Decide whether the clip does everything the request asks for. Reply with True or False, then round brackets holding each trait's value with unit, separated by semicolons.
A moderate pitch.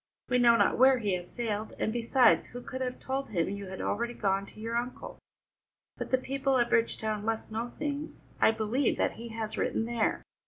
False (230 Hz)